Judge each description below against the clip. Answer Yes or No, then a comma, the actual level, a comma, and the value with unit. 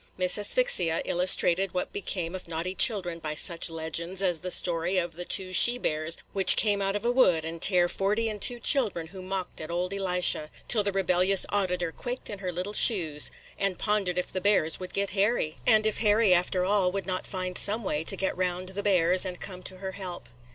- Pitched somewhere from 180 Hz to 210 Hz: Yes, medium, 185 Hz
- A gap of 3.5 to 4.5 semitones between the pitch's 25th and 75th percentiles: No, narrow, 2.4 semitones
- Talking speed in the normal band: No, fast, 215 wpm